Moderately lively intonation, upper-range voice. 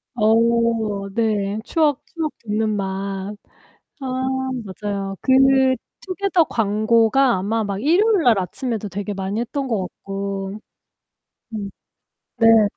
Yes: average, 4.0 semitones; high, 215 Hz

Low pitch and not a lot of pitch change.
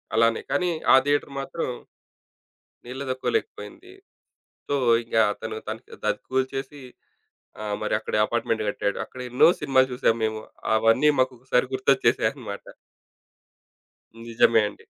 No: low, 130 Hz; average, 3.3 semitones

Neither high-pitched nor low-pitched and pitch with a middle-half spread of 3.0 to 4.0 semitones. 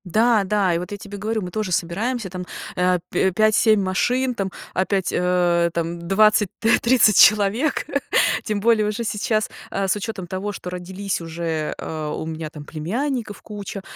No: high, 195 Hz; average, 3.4 semitones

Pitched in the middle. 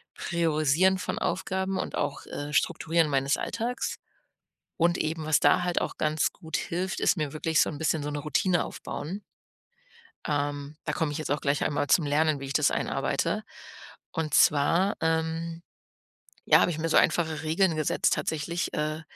Yes: medium, 160 Hz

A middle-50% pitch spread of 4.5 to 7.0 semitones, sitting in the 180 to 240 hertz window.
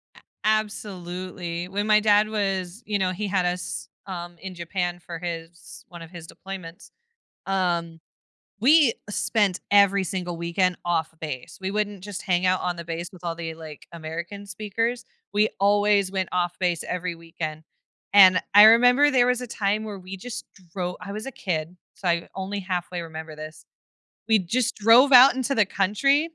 No: average, 3.4 semitones; medium, 185 Hz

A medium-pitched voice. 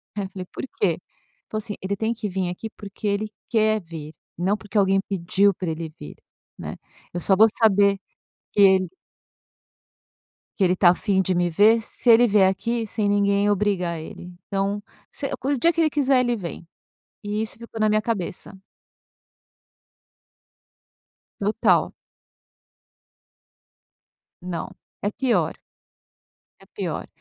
No: high, 200 Hz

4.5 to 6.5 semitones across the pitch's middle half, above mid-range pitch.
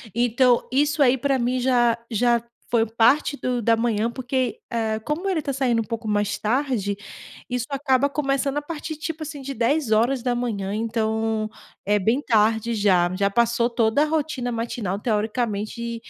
No: average, 3.4 semitones; high, 235 Hz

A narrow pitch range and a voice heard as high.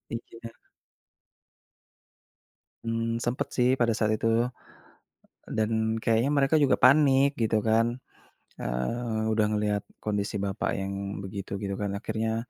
No: narrow, 2.1 semitones; low, 115 Hz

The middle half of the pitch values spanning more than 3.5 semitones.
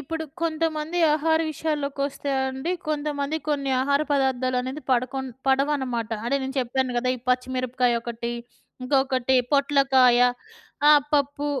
No: narrow, 2.5 semitones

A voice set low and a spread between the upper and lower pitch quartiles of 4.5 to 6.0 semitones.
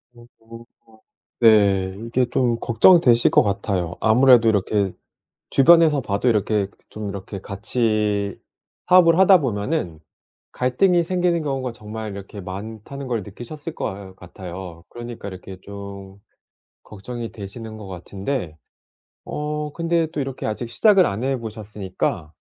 Yes: low, 110 Hz; average, 5.2 semitones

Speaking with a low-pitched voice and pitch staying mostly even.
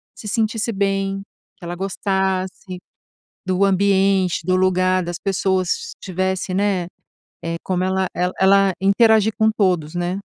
No: high, 190 Hz; narrow, 1.2 semitones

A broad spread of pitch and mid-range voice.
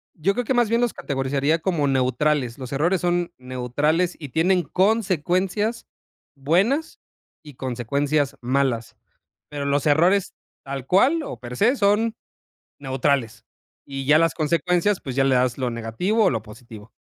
Yes: wide, 6.0 semitones; medium, 150 Hz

